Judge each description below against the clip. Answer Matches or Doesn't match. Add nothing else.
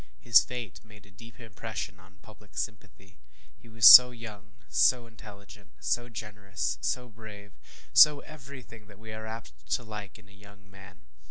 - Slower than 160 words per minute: Doesn't match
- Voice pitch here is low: Matches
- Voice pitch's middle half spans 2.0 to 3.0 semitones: Matches